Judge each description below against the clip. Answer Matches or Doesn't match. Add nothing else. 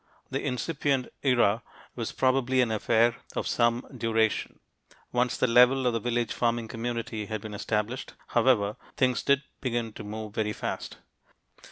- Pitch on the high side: Doesn't match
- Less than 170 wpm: Matches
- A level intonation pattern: Matches